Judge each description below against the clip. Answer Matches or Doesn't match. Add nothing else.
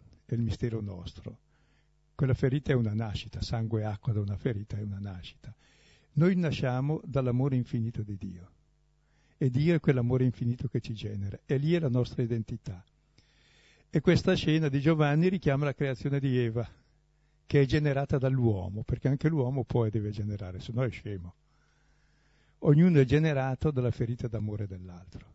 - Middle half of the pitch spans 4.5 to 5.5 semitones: Matches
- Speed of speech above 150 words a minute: Matches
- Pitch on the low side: Matches